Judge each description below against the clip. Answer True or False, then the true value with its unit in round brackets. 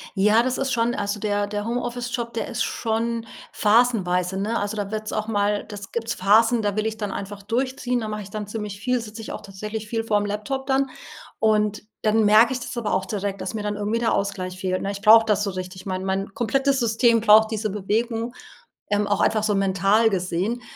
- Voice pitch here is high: True (215 Hz)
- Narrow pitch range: True (2.3 semitones)